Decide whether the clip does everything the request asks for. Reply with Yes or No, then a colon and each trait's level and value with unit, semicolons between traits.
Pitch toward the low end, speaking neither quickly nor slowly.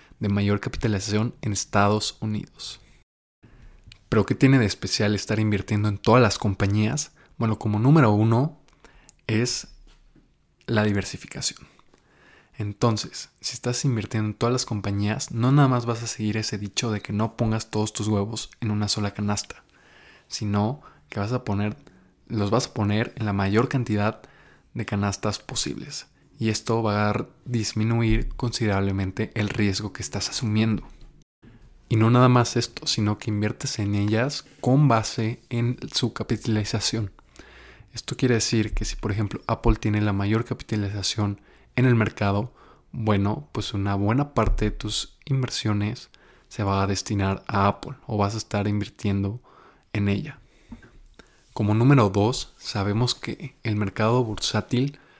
Yes: low, 110 Hz; average, 150 wpm